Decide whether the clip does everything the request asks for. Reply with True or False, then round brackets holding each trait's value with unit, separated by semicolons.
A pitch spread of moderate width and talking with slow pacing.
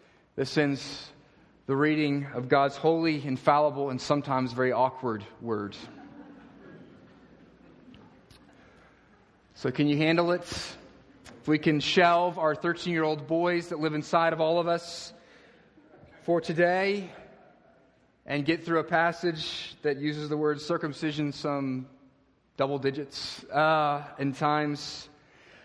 True (3.1 semitones; 115 wpm)